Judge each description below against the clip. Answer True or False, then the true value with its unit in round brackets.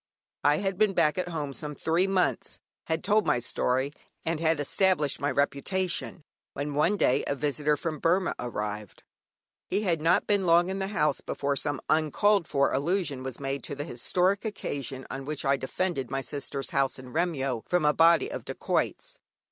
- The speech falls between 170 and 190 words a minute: True (180 wpm)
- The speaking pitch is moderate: True (150 Hz)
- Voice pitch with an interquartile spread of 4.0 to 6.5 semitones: True (4.8 semitones)